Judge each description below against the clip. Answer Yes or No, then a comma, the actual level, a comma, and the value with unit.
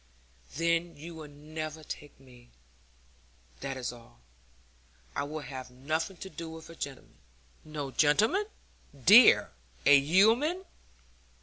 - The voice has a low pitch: No, medium, 155 Hz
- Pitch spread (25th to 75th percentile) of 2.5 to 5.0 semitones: Yes, average, 3.5 semitones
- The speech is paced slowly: Yes, slow, 120 wpm